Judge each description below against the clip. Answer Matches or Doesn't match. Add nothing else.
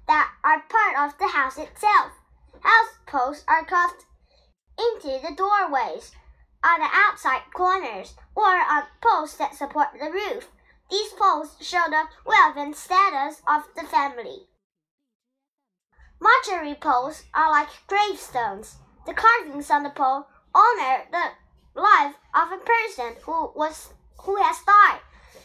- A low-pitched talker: Doesn't match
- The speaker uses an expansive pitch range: Matches